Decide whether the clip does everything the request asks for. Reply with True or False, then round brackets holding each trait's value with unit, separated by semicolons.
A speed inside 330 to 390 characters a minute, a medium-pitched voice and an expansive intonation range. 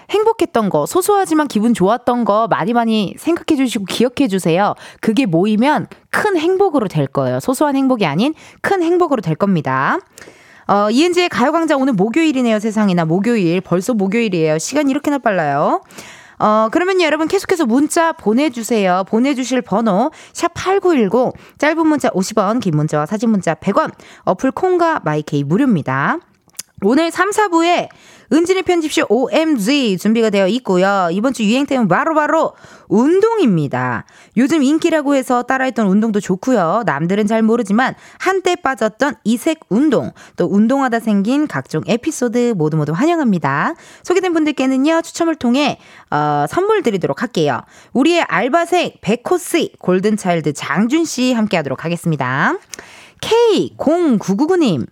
False (335 characters per minute; 245 Hz; 8.5 semitones)